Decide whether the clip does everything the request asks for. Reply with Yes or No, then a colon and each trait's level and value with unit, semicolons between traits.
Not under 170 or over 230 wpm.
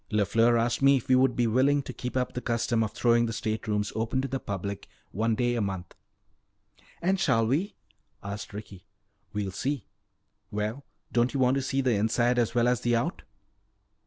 Yes: average, 195 wpm